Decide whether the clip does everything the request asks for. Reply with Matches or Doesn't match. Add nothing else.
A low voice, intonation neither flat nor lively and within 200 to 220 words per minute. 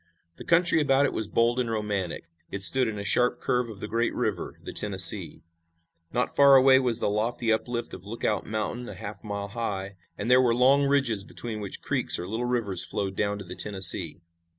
Matches